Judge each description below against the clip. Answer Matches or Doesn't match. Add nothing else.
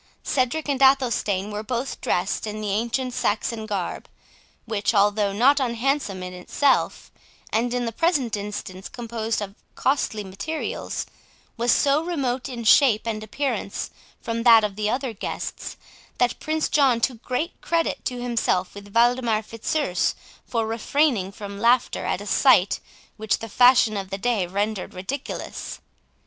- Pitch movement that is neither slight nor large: Matches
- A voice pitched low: Doesn't match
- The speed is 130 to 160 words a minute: Matches